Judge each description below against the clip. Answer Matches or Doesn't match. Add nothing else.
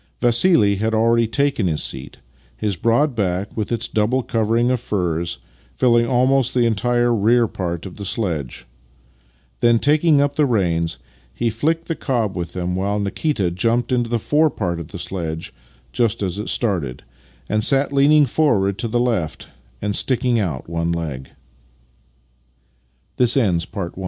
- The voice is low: Matches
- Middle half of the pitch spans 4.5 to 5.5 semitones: Matches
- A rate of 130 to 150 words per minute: Matches